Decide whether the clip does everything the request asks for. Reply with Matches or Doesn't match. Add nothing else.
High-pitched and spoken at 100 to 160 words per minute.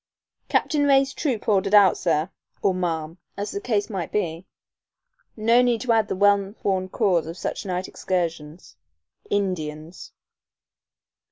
Matches